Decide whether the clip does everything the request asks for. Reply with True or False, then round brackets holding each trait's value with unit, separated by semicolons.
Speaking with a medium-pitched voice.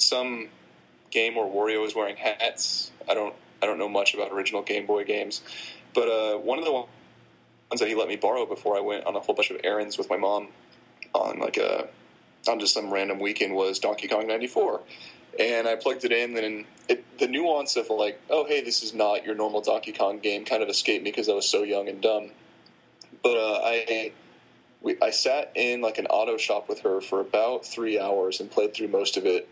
False (115 Hz)